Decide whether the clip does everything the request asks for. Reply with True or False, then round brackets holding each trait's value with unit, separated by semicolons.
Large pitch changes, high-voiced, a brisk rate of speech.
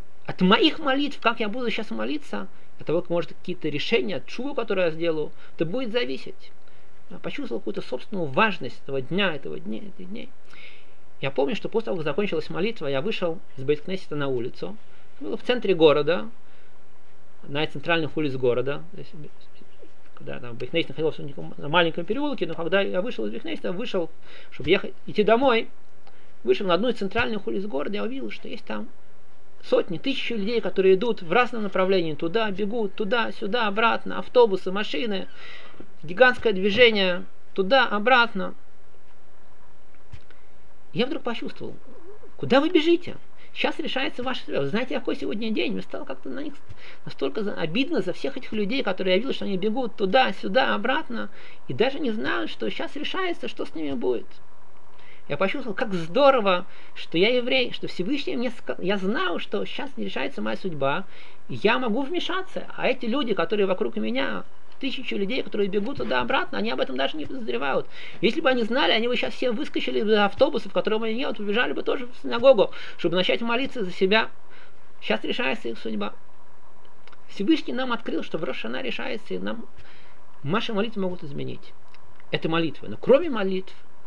True (5.8 semitones; 220 Hz; 170 wpm)